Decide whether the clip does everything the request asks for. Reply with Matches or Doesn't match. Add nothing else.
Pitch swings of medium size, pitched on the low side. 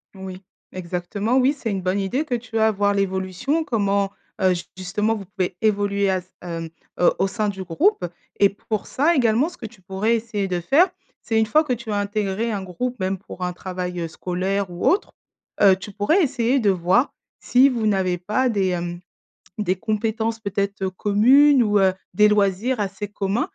Doesn't match